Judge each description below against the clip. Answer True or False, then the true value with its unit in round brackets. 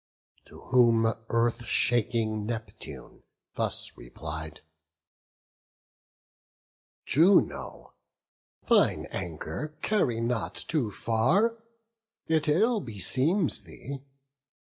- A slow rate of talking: True (75 wpm)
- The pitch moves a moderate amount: False (5.9 semitones)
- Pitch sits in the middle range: False (120 Hz)